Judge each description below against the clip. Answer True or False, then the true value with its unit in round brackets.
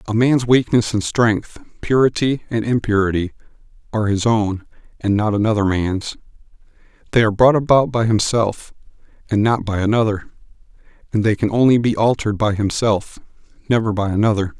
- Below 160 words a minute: True (150 wpm)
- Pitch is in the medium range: False (110 Hz)